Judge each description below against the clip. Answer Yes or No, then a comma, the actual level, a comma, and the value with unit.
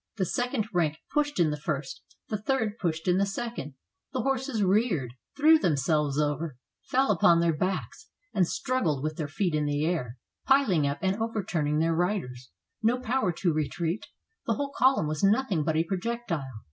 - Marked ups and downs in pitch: Yes, wide, 6.9 semitones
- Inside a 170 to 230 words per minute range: Yes, average, 175 wpm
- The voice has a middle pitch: Yes, medium, 180 Hz